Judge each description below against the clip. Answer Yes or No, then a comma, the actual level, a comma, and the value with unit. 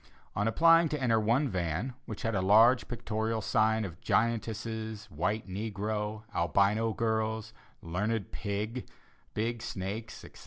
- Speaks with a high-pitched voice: No, low, 110 Hz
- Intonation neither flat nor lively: No, narrow, 1.8 semitones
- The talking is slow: Yes, slow, 130 wpm